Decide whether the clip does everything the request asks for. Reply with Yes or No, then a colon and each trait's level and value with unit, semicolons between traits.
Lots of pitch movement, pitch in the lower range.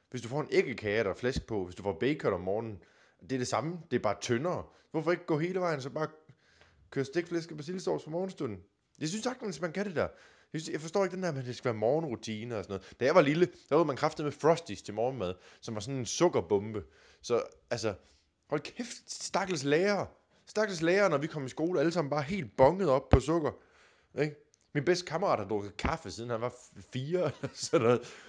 No: wide, 7.0 semitones; medium, 150 Hz